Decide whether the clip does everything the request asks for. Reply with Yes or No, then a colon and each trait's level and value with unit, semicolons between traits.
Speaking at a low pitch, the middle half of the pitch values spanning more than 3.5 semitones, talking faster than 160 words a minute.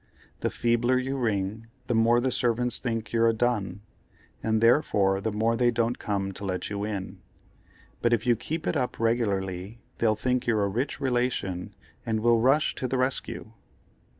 No: low, 115 Hz; average, 3.0 semitones; average, 175 wpm